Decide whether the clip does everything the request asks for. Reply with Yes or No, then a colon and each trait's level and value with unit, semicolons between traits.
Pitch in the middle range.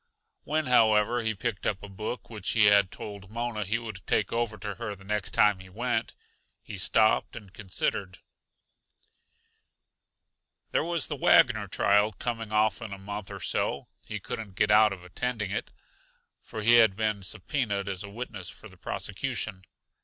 No: low, 105 Hz